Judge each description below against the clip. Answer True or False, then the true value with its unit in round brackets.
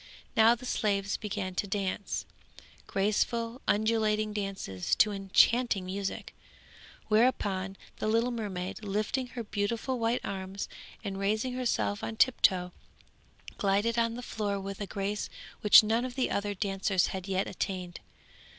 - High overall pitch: True (205 Hz)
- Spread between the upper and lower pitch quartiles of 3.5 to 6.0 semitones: False (2.8 semitones)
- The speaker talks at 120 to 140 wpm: True (135 wpm)